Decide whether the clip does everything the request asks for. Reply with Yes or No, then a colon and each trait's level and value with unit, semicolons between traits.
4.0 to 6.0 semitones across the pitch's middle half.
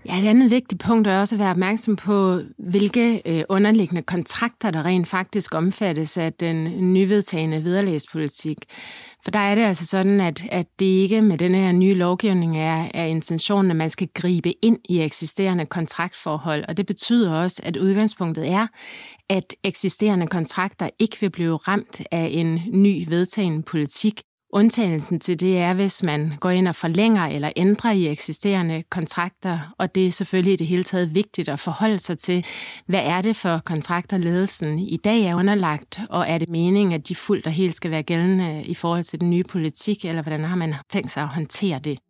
No: average, 3.2 semitones